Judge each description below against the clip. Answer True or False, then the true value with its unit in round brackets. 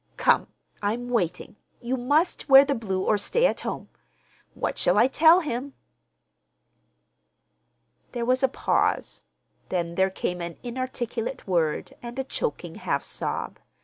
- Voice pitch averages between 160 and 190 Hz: False (240 Hz)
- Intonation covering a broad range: True (5.8 semitones)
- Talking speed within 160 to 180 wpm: False (140 wpm)